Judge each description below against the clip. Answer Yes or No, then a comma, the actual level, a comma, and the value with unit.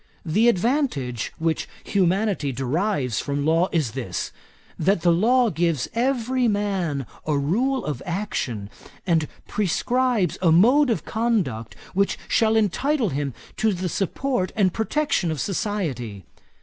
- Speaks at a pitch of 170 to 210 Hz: Yes, medium, 185 Hz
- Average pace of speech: No, slow, 130 wpm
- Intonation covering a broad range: Yes, wide, 7.2 semitones